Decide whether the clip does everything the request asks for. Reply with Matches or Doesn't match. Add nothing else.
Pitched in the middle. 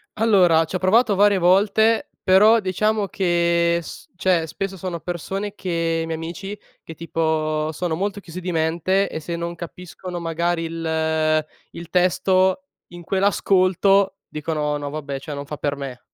Matches